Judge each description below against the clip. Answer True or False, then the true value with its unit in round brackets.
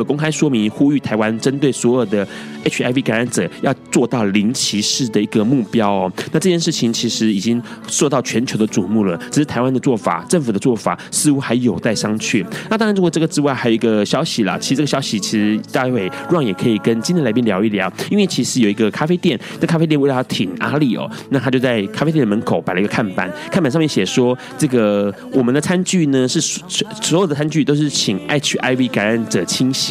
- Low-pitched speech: True (130 Hz)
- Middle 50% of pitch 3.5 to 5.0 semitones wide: False (5.6 semitones)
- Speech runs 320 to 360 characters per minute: True (350 characters per minute)